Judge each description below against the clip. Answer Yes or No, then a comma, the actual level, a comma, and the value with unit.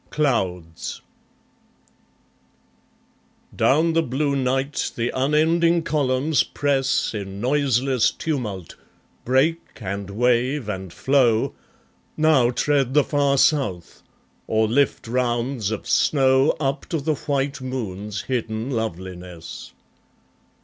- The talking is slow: Yes, slow, 100 wpm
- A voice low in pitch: Yes, low, 130 Hz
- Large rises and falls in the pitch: No, average, 4.5 semitones